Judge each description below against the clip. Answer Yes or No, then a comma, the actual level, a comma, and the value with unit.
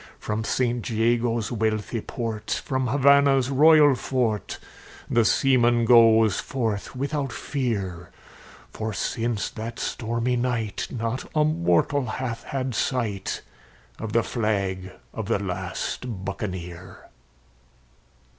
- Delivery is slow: Yes, slow, 110 wpm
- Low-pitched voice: Yes, low, 115 Hz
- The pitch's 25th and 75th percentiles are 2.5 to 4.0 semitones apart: Yes, average, 3.2 semitones